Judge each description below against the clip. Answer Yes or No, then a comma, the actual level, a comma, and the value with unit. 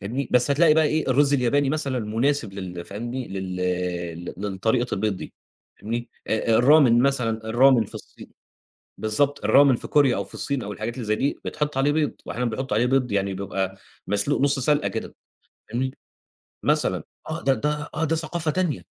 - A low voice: Yes, low, 125 Hz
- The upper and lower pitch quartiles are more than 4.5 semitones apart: Yes, wide, 5.5 semitones